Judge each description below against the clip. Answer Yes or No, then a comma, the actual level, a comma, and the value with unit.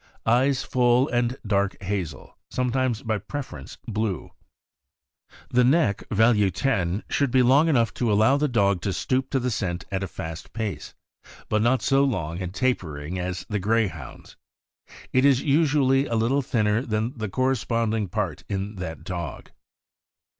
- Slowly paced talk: No, average, 155 wpm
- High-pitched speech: No, low, 110 Hz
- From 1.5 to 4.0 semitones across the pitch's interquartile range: No, average, 4.8 semitones